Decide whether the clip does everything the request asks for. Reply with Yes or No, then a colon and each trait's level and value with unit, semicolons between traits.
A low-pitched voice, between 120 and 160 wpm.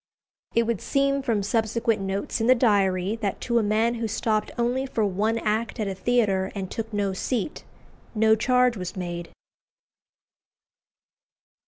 No: high, 220 Hz; average, 155 wpm